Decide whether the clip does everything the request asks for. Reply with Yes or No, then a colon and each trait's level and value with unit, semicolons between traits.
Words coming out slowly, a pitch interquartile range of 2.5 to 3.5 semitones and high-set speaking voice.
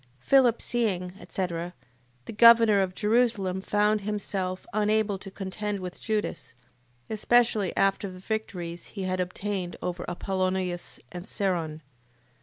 Yes: slow, 120 wpm; average, 2.8 semitones; high, 195 Hz